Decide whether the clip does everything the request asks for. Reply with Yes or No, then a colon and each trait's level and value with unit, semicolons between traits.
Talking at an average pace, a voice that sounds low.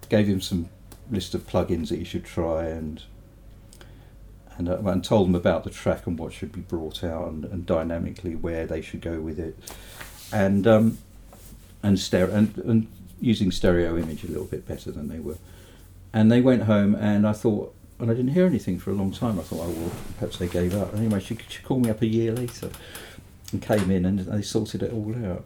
No: fast, 220 wpm; very low, 95 Hz